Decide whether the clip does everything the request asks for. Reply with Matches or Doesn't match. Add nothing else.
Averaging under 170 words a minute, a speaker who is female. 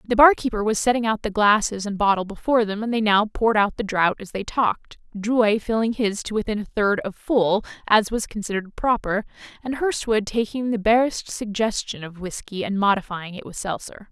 Doesn't match